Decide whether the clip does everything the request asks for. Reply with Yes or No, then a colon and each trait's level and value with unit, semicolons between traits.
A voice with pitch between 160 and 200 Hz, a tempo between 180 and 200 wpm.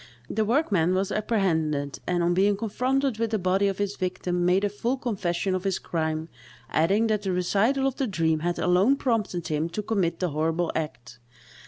Yes: high, 190 Hz; average, 190 wpm